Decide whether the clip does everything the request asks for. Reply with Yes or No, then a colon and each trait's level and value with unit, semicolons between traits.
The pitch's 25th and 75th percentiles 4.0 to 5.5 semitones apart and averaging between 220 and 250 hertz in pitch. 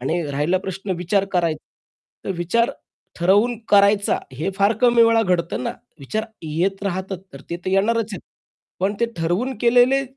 No: average, 4.5 semitones; high, 195 Hz